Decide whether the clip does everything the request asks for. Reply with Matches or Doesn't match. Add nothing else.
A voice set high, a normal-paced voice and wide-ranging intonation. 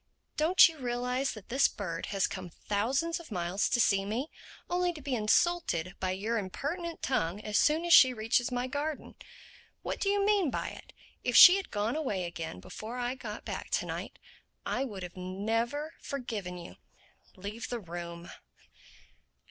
Matches